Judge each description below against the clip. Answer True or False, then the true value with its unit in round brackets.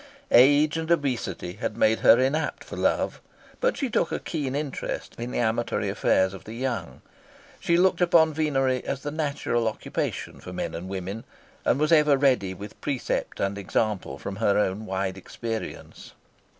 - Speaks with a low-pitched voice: True (125 Hz)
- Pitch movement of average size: False (6.6 semitones)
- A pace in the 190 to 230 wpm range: False (170 wpm)